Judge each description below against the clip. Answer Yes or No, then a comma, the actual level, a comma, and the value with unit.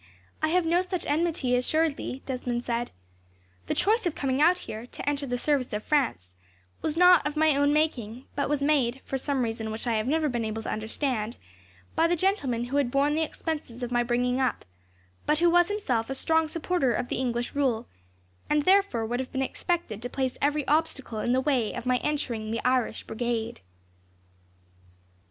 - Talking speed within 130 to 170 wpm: No, average, 195 wpm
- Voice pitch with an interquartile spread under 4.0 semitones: No, average, 4.3 semitones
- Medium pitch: No, very high, 265 Hz